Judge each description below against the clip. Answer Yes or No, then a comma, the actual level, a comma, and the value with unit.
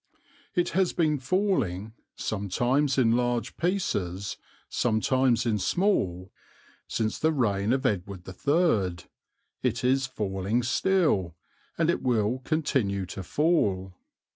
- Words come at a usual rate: No, slow, 115 wpm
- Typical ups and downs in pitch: No, wide, 7.1 semitones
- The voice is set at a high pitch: No, low, 120 Hz